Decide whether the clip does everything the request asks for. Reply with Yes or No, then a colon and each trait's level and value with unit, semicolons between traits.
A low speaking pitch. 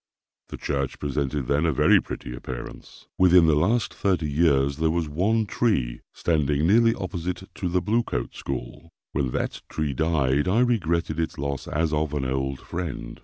Yes: very low, 80 Hz